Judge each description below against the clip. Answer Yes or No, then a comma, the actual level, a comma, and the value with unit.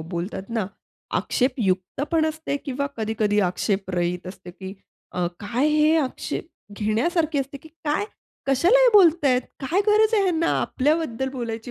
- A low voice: No, very high, 265 Hz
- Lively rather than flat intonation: Yes, wide, 7.4 semitones